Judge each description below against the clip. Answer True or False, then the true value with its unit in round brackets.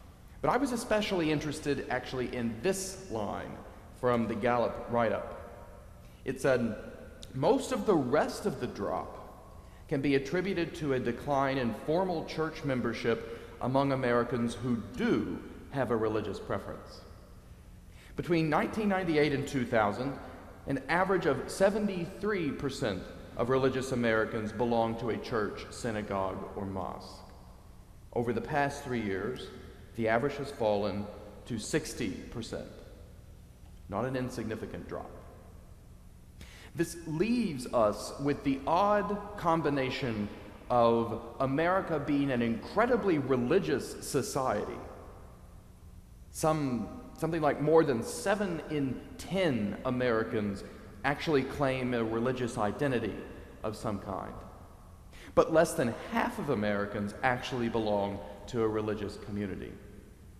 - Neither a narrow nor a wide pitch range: False (5.9 semitones)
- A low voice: True (125 Hz)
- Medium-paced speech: False (115 wpm)